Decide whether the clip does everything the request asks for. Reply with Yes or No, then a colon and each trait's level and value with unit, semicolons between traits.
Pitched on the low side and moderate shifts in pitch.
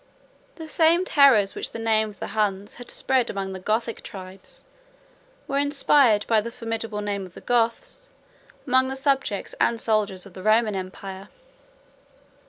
No: high, 220 Hz; average, 4.7 semitones